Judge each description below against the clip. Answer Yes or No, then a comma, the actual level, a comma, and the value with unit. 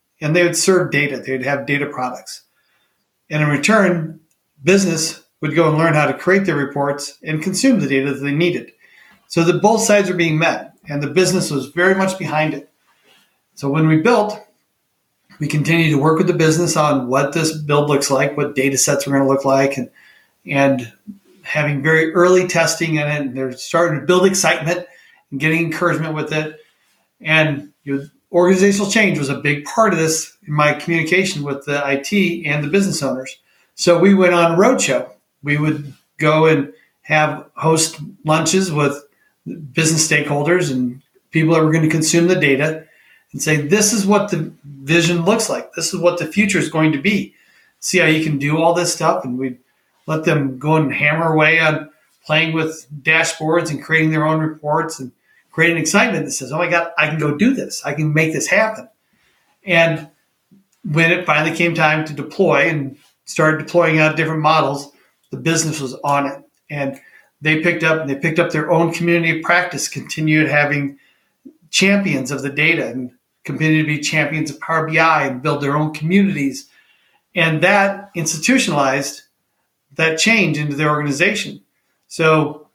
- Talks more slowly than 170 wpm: No, average, 185 wpm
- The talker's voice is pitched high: No, medium, 160 Hz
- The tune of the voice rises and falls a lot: No, average, 3.0 semitones